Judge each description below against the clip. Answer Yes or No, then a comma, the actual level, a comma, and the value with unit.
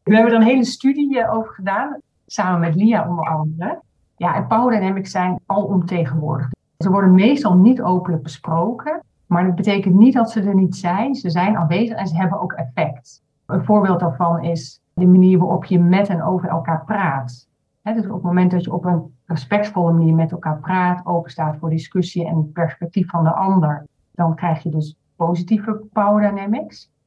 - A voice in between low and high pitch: Yes, medium, 180 Hz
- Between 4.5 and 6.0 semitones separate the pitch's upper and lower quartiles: No, average, 3.9 semitones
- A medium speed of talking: Yes, average, 185 wpm